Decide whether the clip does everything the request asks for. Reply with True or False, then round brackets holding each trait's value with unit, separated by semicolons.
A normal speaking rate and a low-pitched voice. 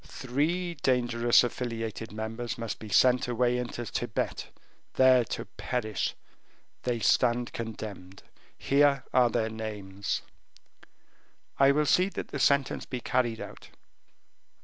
False (120 wpm; 120 Hz)